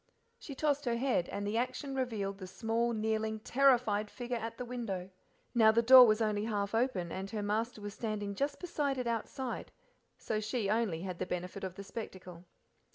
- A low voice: No, high, 220 Hz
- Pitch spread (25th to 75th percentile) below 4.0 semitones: Yes, average, 3.4 semitones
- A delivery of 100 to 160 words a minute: No, average, 190 wpm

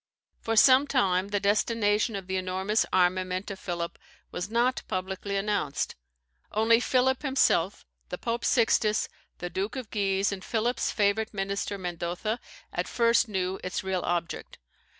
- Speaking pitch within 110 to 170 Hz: No, high, 200 Hz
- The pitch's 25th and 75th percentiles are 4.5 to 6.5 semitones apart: No, average, 3.4 semitones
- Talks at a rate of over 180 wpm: No, average, 145 wpm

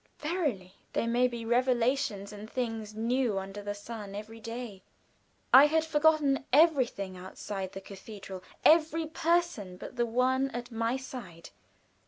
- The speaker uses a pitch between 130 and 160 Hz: No, high, 235 Hz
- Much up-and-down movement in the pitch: No, average, 4.9 semitones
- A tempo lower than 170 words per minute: Yes, average, 140 wpm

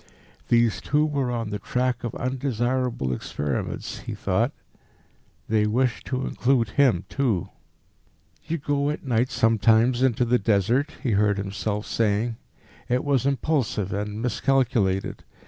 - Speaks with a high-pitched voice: No, low, 120 Hz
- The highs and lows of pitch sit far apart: No, average, 3.8 semitones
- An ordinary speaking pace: No, slow, 130 wpm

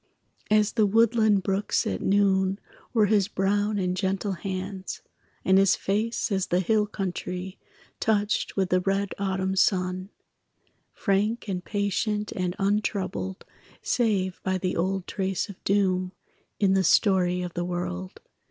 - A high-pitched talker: Yes, high, 195 Hz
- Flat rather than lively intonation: Yes, narrow, 1.9 semitones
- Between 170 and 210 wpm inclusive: No, average, 140 wpm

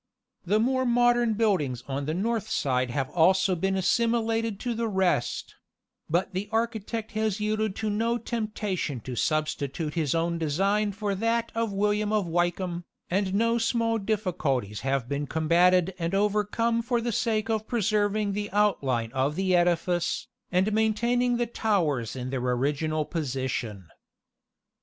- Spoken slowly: No, average, 145 wpm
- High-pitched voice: Yes, high, 195 Hz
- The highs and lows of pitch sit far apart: Yes, wide, 6.0 semitones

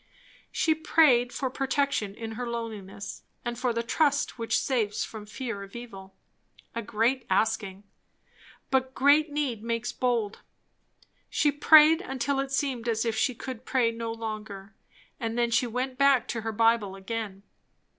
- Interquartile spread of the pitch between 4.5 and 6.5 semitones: No, average, 3.2 semitones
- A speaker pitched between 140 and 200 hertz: No, high, 235 Hz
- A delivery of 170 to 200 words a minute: No, average, 155 wpm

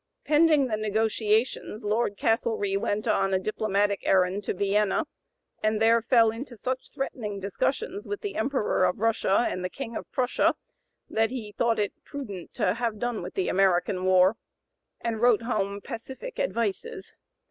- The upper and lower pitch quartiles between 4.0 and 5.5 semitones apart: No, average, 3.4 semitones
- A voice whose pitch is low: No, high, 220 Hz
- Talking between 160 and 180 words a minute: Yes, average, 165 wpm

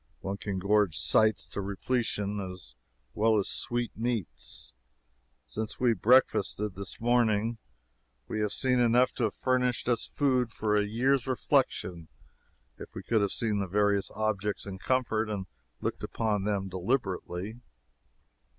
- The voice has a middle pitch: No, low, 105 Hz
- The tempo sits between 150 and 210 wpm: No, average, 140 wpm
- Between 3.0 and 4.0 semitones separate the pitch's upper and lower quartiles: Yes, average, 3.3 semitones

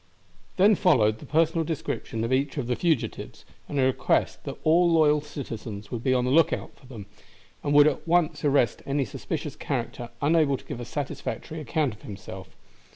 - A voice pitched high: No, medium, 140 Hz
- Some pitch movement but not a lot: Yes, average, 4.6 semitones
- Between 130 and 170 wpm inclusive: No, average, 190 wpm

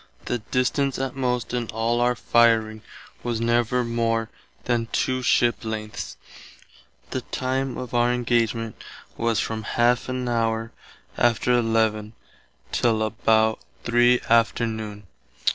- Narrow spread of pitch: Yes, narrow, 1.6 semitones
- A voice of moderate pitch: No, low, 115 Hz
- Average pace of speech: No, slow, 120 wpm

